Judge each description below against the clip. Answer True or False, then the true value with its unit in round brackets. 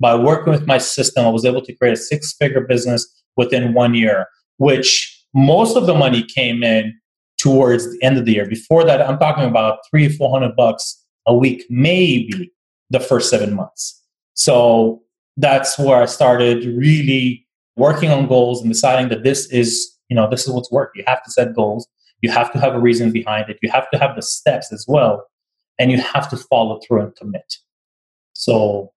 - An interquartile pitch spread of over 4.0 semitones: False (2.5 semitones)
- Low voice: True (125 Hz)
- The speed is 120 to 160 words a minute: False (200 wpm)